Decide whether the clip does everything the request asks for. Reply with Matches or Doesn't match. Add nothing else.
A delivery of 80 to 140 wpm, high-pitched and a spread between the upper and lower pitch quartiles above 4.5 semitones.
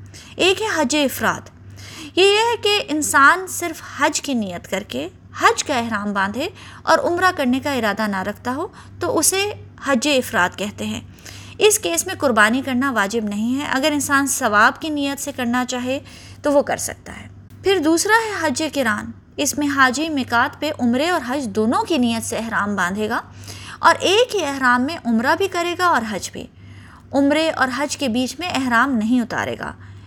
Doesn't match